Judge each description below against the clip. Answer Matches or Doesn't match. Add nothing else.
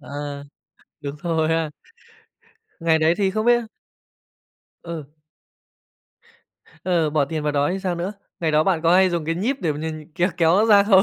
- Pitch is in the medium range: Matches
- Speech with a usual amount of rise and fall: Matches